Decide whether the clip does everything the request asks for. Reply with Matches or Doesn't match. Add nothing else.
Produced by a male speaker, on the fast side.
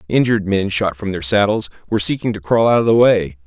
Matches